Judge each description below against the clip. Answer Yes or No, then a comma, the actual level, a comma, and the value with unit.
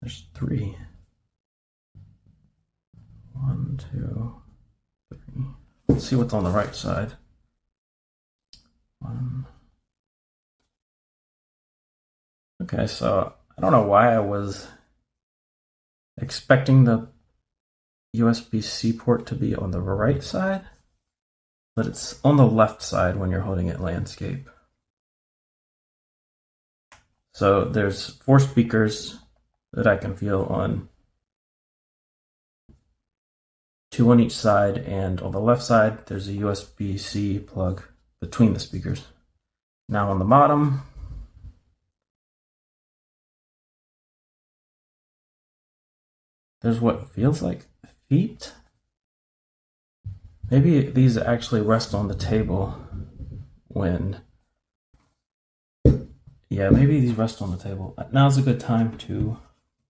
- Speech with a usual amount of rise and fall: Yes, average, 4.6 semitones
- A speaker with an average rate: No, slow, 100 wpm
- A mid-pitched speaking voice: No, low, 105 Hz